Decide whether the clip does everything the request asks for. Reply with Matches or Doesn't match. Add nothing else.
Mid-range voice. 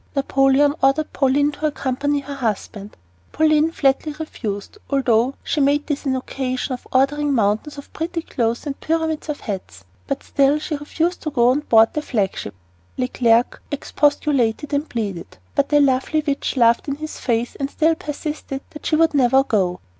Doesn't match